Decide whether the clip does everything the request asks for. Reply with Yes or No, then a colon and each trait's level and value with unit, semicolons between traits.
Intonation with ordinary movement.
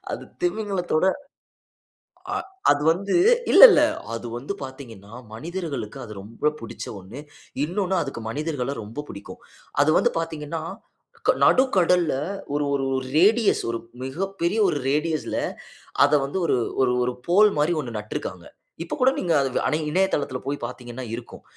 No: wide, 6.0 semitones